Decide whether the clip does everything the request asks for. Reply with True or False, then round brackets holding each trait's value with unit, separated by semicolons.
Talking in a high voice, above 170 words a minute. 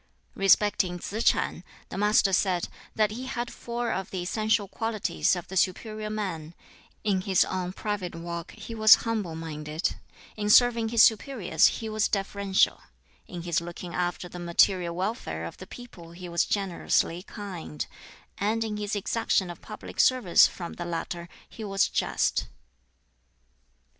False (195 Hz; 155 wpm)